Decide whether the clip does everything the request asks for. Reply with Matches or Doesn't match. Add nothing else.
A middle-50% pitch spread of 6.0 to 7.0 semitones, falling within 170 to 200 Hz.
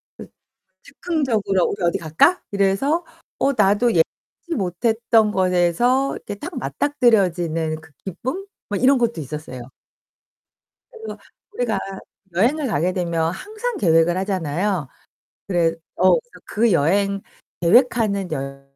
Matches